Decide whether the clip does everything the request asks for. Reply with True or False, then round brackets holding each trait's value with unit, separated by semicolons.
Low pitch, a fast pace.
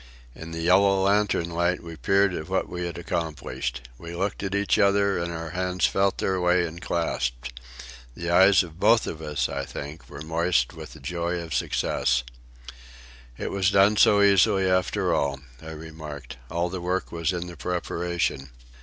False (85 Hz; 180 wpm)